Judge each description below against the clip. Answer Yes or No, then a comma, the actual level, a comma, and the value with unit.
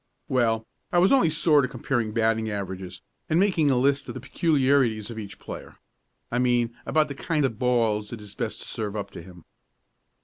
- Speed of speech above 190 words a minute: Yes, average, 200 wpm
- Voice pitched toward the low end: Yes, low, 120 Hz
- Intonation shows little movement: No, average, 4.6 semitones